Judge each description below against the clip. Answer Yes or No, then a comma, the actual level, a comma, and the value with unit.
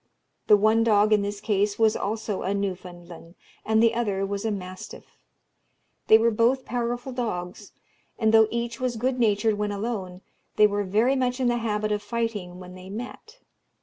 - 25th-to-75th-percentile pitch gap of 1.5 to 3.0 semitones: Yes, average, 2.7 semitones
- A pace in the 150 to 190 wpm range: Yes, average, 180 wpm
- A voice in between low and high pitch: No, high, 215 Hz